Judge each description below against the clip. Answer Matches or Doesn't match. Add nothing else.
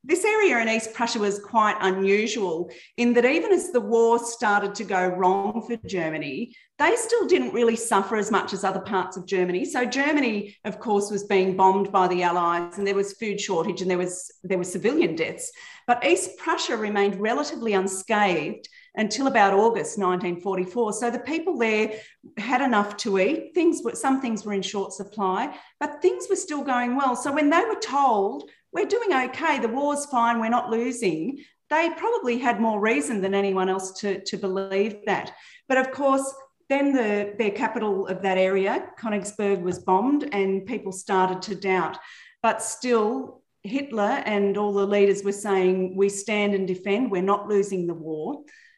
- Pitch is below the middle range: Doesn't match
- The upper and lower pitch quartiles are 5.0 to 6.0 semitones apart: Matches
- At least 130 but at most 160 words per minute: Doesn't match